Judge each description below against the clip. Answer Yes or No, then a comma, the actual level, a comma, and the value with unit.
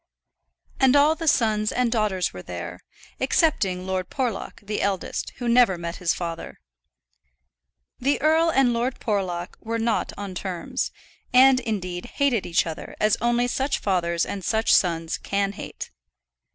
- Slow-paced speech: No, average, 150 wpm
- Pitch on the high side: Yes, high, 210 Hz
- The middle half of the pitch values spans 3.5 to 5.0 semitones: No, wide, 5.5 semitones